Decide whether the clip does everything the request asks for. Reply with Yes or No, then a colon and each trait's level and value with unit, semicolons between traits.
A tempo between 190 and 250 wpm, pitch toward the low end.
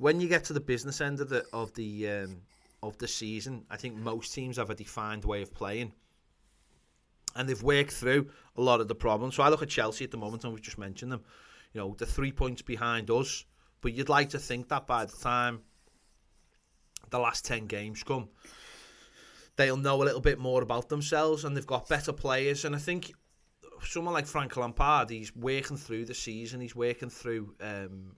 Yes: fast, 205 wpm; low, 125 Hz